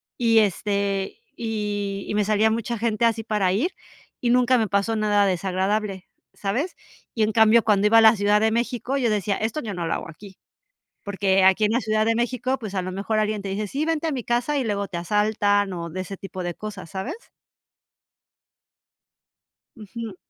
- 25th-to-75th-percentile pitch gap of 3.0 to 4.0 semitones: No, narrow, 2.5 semitones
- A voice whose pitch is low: No, high, 210 Hz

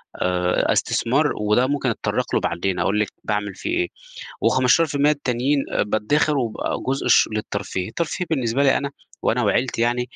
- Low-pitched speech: Yes, low, 125 Hz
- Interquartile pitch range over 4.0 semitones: Yes, average, 5.1 semitones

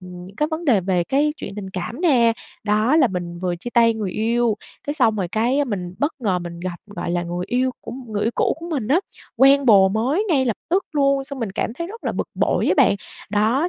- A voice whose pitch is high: Yes, high, 230 Hz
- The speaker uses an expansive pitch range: Yes, wide, 6.5 semitones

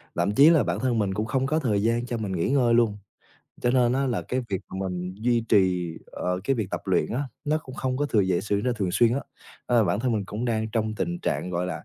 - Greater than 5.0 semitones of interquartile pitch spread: No, average, 4.7 semitones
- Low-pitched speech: Yes, low, 115 Hz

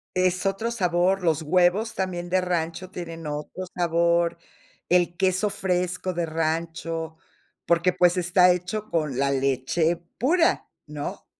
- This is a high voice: No, medium, 175 Hz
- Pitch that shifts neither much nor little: No, narrow, 2.0 semitones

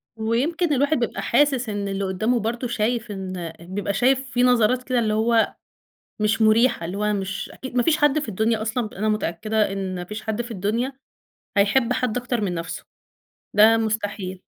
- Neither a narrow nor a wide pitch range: Yes, average, 3.5 semitones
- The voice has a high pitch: Yes, high, 220 Hz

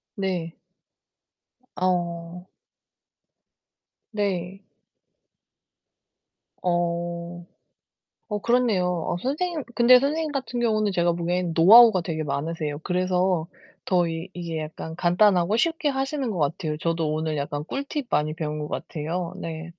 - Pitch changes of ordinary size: Yes, average, 4.5 semitones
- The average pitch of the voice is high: No, medium, 175 Hz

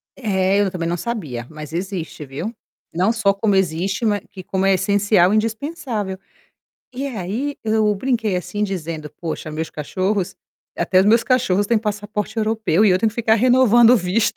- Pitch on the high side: Yes, high, 205 Hz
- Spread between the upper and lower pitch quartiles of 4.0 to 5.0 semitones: No, average, 3.5 semitones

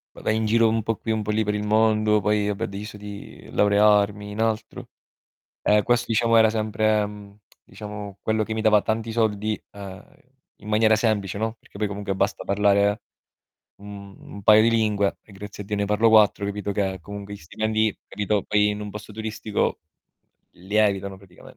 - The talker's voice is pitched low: Yes, low, 105 Hz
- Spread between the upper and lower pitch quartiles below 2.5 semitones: Yes, narrow, 1.3 semitones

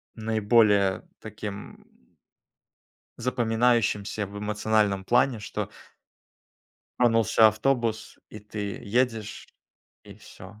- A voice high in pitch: No, low, 110 Hz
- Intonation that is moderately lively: No, narrow, 1.9 semitones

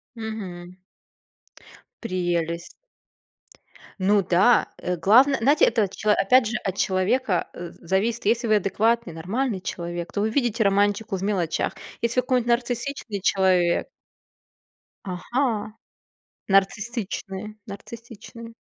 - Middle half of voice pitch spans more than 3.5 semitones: Yes, average, 4.0 semitones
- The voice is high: Yes, high, 210 Hz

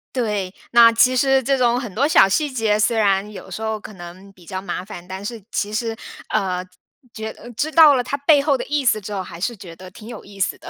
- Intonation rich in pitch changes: No, average, 4.6 semitones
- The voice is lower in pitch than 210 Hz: No, high, 215 Hz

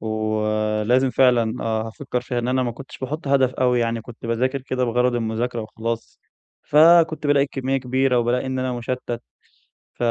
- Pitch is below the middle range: Yes, low, 125 Hz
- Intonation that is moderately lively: No, narrow, 2.2 semitones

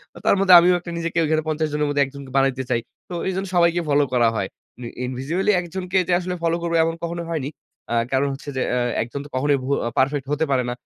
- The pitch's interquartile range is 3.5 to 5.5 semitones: Yes, average, 4.2 semitones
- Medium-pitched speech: Yes, medium, 150 Hz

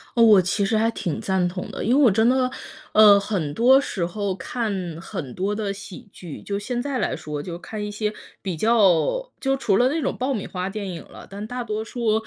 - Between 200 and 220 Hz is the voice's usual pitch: Yes, high, 210 Hz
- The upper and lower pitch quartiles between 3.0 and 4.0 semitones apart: Yes, average, 3.7 semitones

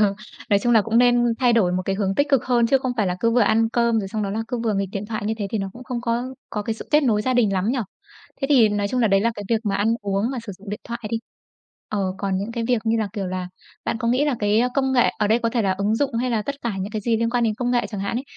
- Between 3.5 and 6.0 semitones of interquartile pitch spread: No, average, 2.9 semitones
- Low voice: No, high, 225 Hz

